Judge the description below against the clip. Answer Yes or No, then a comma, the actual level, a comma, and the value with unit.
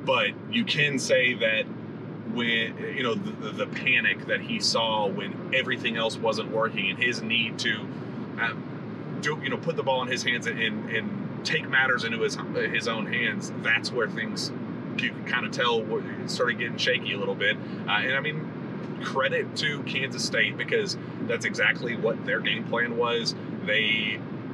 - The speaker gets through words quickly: No, average, 180 wpm